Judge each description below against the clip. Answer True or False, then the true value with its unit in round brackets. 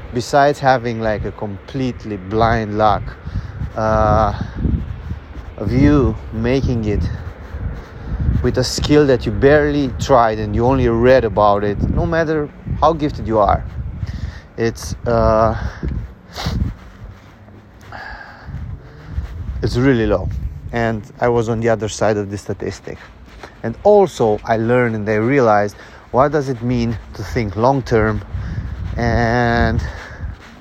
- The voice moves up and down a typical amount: True (3.6 semitones)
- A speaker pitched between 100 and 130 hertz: True (110 Hz)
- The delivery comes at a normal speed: False (120 wpm)